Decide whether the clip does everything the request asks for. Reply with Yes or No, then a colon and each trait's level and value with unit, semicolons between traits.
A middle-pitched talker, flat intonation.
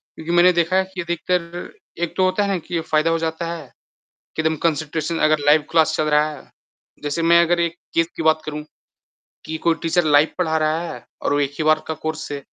Yes: medium, 160 Hz; narrow, 1.7 semitones